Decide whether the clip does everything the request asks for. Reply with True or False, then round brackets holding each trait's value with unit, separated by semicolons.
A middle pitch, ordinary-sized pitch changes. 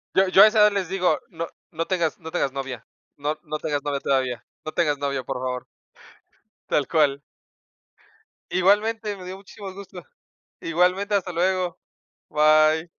True (165 Hz; 4.6 semitones)